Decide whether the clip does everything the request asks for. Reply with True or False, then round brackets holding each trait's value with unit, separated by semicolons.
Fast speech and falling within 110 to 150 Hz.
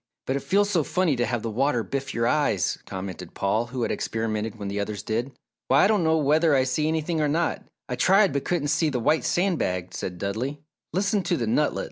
True (230 wpm; 140 Hz)